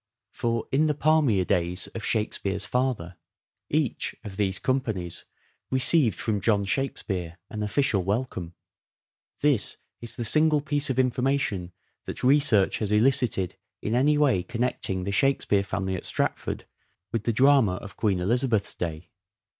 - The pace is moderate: Yes, average, 145 wpm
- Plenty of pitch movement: Yes, wide, 5.8 semitones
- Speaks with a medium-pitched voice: No, low, 110 Hz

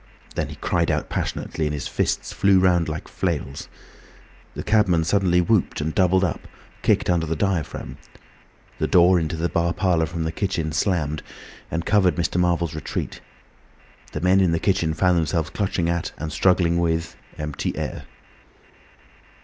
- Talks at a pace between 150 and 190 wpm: Yes, average, 160 wpm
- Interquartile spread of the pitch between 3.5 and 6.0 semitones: No, narrow, 2.4 semitones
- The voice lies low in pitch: Yes, very low, 85 Hz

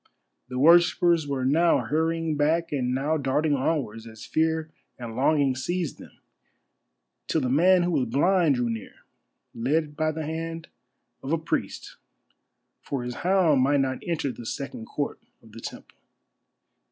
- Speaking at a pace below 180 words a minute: Yes, average, 155 wpm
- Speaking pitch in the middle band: Yes, medium, 150 Hz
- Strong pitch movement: No, average, 4.0 semitones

